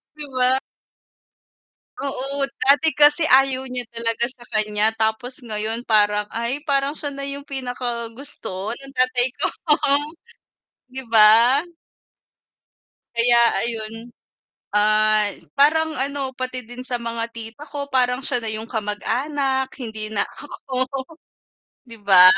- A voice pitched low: No, high, 245 Hz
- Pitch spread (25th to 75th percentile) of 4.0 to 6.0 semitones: No, average, 3.6 semitones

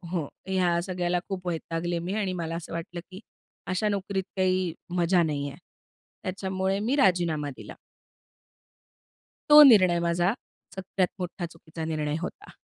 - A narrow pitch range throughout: Yes, narrow, 2.2 semitones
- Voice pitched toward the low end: No, medium, 180 Hz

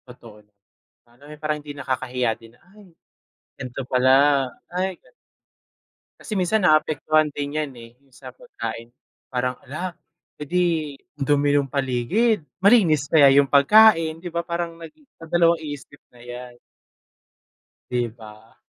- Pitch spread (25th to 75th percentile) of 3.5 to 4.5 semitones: No, average, 5.0 semitones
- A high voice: No, medium, 145 Hz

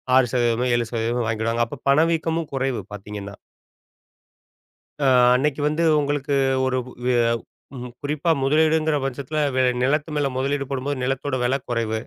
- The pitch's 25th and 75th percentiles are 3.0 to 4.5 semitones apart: Yes, average, 3.5 semitones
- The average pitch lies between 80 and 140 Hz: Yes, low, 135 Hz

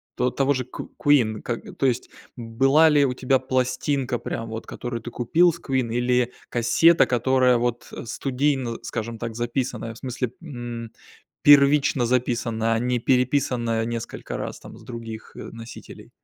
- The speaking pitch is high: No, low, 125 Hz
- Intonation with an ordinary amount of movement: No, narrow, 2.3 semitones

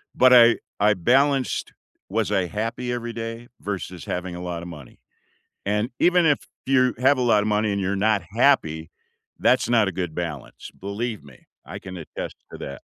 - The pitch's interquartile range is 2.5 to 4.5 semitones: No, average, 5.0 semitones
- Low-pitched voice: Yes, low, 105 Hz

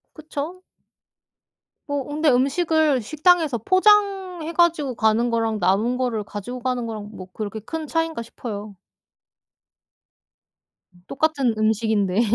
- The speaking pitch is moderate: No, very high, 255 Hz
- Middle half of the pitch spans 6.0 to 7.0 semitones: Yes, wide, 6.5 semitones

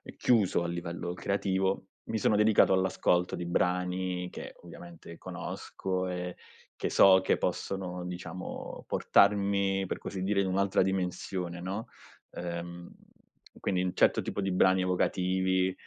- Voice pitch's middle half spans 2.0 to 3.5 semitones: No, narrow, 1.3 semitones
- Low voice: Yes, very low, 95 Hz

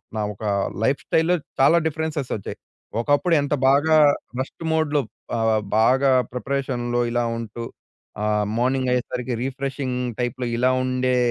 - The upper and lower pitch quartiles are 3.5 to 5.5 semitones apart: No, average, 2.7 semitones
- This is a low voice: Yes, low, 130 Hz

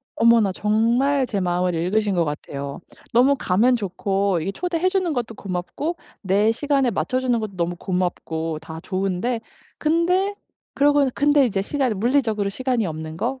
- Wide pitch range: Yes, wide, 6.5 semitones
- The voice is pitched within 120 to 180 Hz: No, high, 220 Hz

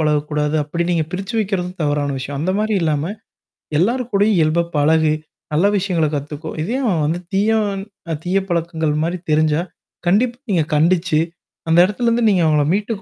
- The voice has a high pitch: No, medium, 170 Hz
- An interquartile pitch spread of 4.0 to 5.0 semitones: Yes, average, 4.4 semitones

